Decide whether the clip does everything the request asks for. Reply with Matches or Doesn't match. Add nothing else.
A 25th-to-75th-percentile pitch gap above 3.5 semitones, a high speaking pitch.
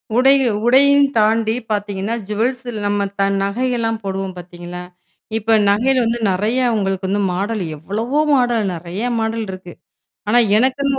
Matches